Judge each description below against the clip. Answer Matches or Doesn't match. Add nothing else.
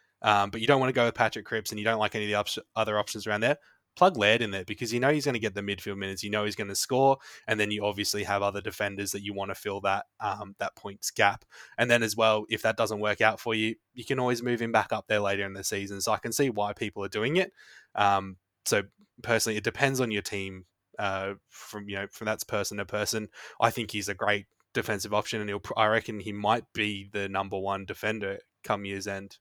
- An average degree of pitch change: Doesn't match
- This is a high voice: Doesn't match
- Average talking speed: Doesn't match